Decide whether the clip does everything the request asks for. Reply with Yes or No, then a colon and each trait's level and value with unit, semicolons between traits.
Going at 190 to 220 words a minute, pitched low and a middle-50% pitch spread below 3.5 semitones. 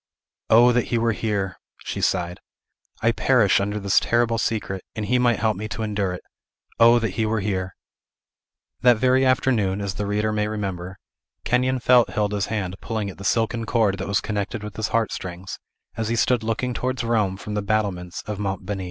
Yes: average, 195 wpm; low, 105 Hz; average, 2.8 semitones